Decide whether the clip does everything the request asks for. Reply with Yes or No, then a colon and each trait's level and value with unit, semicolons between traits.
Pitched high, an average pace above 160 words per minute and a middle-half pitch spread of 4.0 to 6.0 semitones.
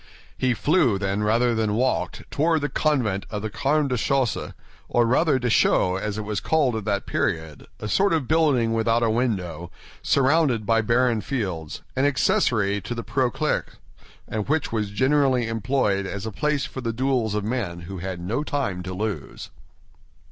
No: low, 115 Hz; average, 170 wpm; average, 4.7 semitones